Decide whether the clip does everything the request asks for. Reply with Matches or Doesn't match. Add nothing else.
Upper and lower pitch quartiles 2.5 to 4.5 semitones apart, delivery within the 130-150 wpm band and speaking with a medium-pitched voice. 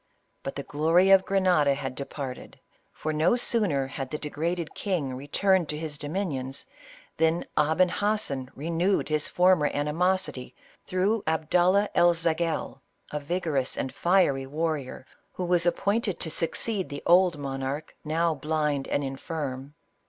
Matches